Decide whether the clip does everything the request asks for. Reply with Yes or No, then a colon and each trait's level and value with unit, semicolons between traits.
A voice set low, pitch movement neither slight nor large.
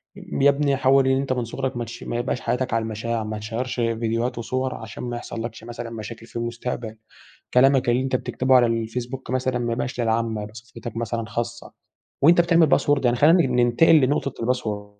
No: low, 120 Hz; narrow, 2.2 semitones